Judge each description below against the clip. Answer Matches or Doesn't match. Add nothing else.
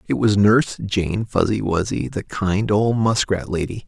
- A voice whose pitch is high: Doesn't match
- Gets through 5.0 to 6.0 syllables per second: Doesn't match